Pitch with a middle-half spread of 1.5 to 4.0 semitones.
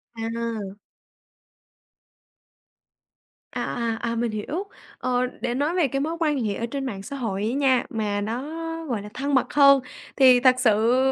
Yes: average, 3.6 semitones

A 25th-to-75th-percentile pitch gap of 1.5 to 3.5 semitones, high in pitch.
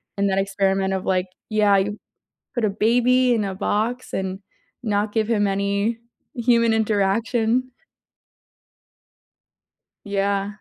Yes: average, 2.7 semitones; high, 205 Hz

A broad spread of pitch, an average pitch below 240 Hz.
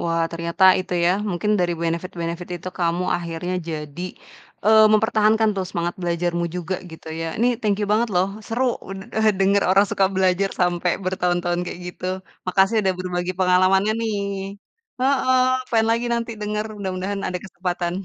No: average, 3.1 semitones; medium, 185 Hz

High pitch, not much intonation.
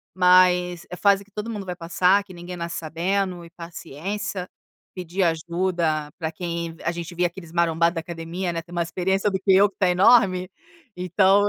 No: medium, 180 Hz; narrow, 2.1 semitones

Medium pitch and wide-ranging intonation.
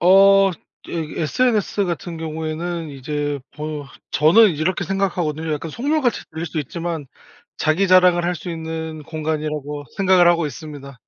No: medium, 160 Hz; average, 3.0 semitones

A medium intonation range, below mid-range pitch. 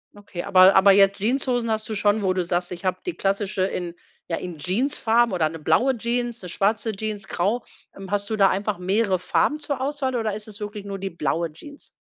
No: average, 3.6 semitones; high, 200 Hz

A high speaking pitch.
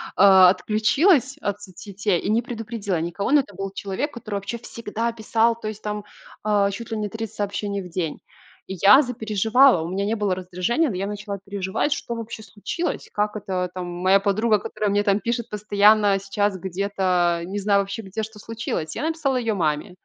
Yes: high, 205 Hz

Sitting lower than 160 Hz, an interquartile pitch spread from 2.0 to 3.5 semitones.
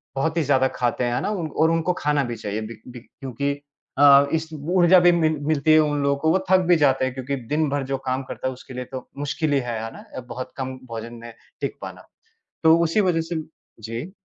No: medium, 140 Hz; average, 3.9 semitones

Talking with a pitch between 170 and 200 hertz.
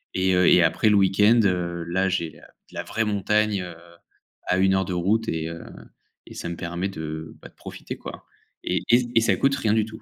No: very low, 95 Hz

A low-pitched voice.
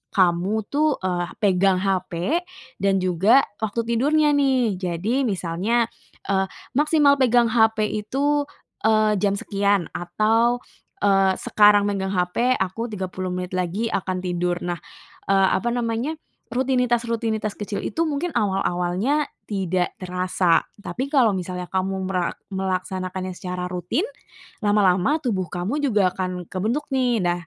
No: high, 200 Hz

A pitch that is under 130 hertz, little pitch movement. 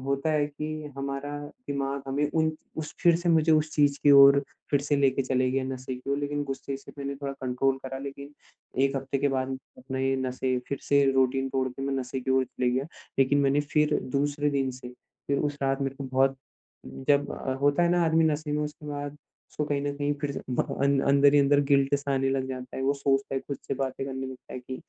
No: medium, 140 Hz; narrow, 1.5 semitones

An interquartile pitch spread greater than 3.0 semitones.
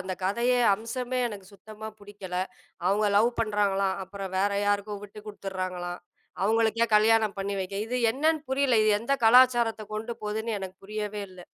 No: narrow, 2.5 semitones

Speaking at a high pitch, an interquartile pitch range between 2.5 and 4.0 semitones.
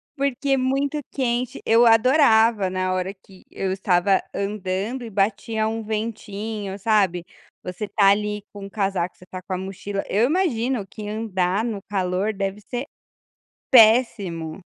Yes: high, 210 Hz; average, 3.1 semitones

